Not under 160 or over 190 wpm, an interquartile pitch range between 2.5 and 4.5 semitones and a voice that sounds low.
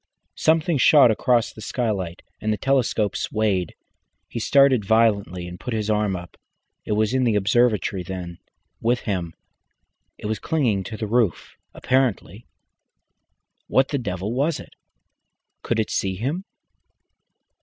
No: average, 140 wpm; average, 4.2 semitones; low, 110 Hz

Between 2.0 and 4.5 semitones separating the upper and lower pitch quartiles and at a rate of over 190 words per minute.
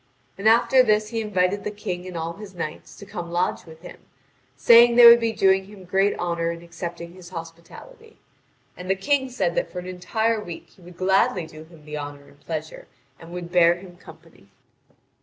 Yes: average, 3.8 semitones; fast, 205 wpm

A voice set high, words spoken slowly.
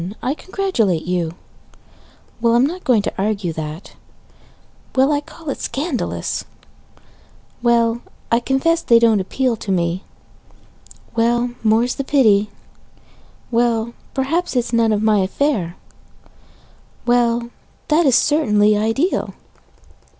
Yes: high, 235 Hz; slow, 120 wpm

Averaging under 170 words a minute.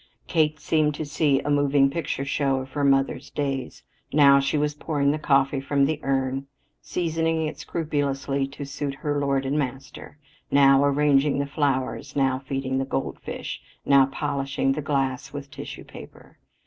Yes: average, 160 wpm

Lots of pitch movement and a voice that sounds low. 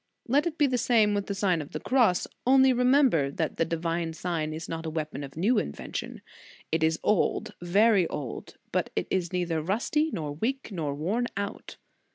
No: wide, 6.8 semitones; medium, 180 Hz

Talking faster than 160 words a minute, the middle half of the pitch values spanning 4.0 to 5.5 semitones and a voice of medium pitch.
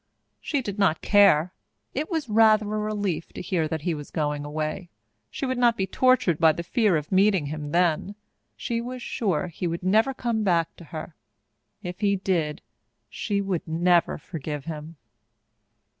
Yes: average, 175 wpm; average, 5.0 semitones; medium, 180 Hz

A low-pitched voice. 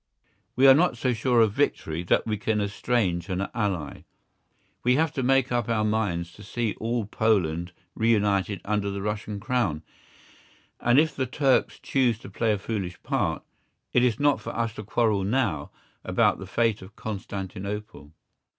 Yes: low, 110 Hz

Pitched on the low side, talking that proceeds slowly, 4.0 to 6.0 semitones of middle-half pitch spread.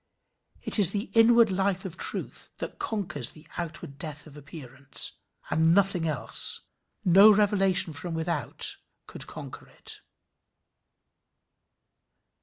No: medium, 175 Hz; slow, 115 wpm; average, 4.5 semitones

